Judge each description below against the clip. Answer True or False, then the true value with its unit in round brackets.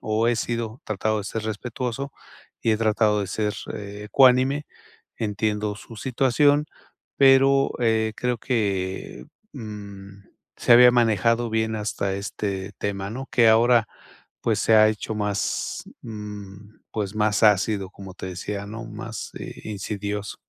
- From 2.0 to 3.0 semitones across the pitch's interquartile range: True (2.4 semitones)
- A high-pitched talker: False (110 Hz)